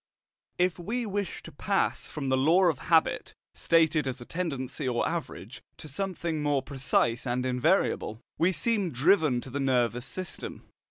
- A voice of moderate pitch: Yes, medium, 150 Hz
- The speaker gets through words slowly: No, average, 160 wpm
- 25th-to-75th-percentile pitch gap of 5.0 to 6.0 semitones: Yes, wide, 5.5 semitones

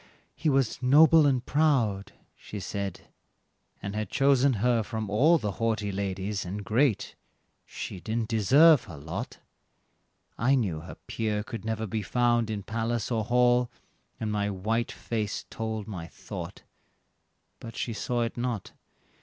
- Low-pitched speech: Yes, low, 110 Hz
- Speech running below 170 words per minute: Yes, average, 145 wpm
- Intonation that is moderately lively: Yes, average, 3.2 semitones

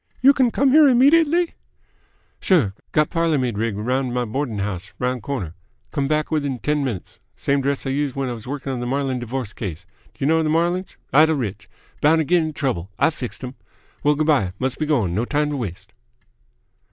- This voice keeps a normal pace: No, fast, 215 wpm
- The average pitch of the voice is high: No, medium, 140 Hz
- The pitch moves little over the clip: No, average, 4.3 semitones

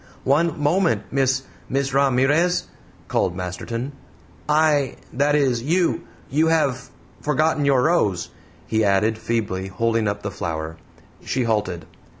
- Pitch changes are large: Yes, wide, 5.9 semitones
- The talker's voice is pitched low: Yes, low, 130 Hz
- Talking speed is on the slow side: Yes, slow, 125 wpm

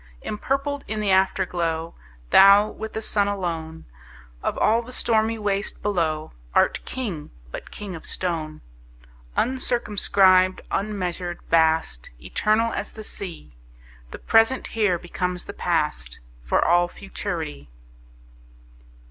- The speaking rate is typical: No, slow, 115 wpm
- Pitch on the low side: No, high, 190 Hz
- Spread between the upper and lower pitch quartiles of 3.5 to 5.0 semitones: Yes, average, 4.4 semitones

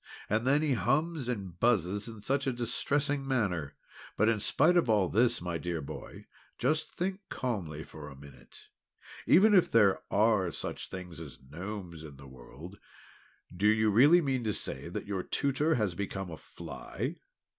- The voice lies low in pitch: Yes, low, 105 Hz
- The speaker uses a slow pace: No, average, 170 wpm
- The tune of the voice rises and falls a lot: Yes, wide, 7.2 semitones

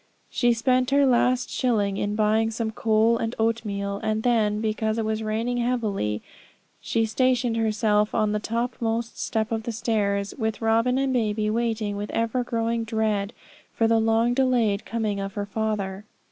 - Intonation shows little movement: Yes, narrow, 1.7 semitones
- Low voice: No, high, 225 Hz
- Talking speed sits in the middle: Yes, average, 165 wpm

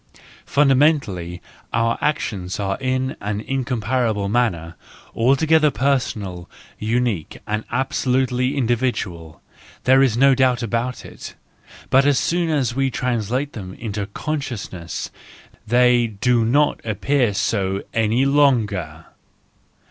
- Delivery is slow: Yes, slow, 110 wpm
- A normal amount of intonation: Yes, average, 4.5 semitones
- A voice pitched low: Yes, low, 120 Hz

